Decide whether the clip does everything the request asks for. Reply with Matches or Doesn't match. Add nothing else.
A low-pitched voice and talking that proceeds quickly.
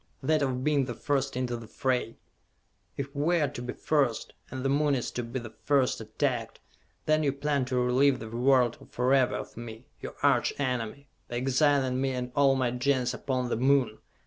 Doesn't match